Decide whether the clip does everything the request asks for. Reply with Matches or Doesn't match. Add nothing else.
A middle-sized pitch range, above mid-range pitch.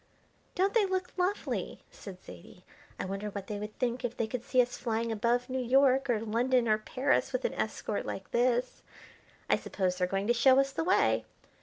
Matches